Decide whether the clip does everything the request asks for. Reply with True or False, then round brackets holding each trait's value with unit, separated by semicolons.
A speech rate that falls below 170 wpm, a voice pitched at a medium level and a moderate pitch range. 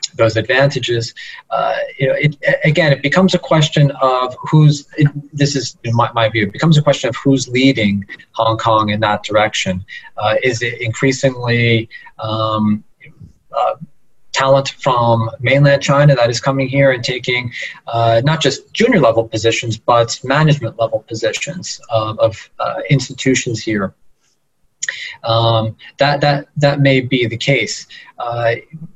False (150 wpm; 130 Hz; 3.8 semitones)